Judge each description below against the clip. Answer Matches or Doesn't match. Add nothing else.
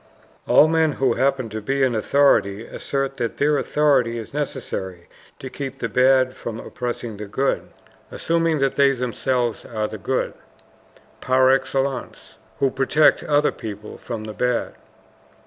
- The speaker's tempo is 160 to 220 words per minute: Doesn't match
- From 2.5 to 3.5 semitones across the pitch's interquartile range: Matches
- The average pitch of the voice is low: Matches